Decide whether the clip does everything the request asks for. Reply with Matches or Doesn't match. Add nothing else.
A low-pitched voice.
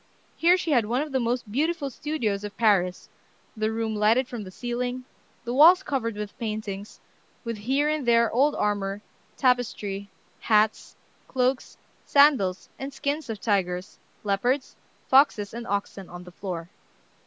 Doesn't match